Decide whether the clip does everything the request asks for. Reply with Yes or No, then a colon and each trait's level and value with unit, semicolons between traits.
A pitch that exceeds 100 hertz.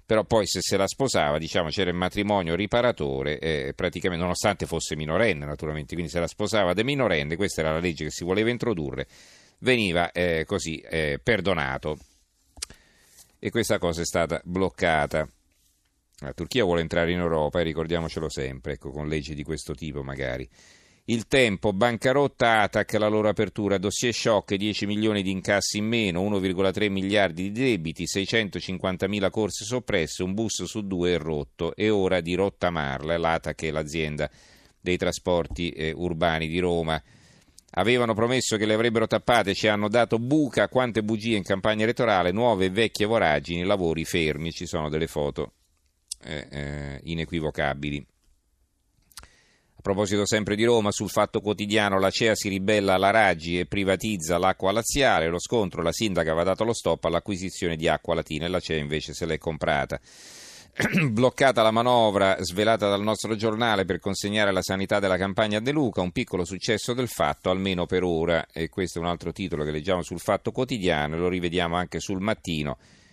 No: very low, 95 Hz